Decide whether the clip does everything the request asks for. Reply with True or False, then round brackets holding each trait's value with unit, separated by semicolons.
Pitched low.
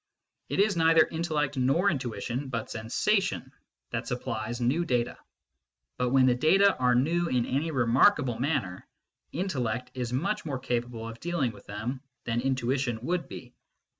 True (130 Hz)